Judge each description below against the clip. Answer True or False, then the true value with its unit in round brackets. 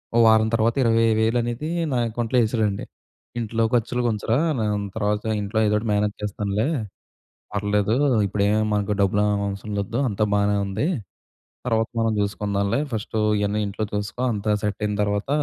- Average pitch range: False (1.7 semitones)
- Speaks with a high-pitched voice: False (105 Hz)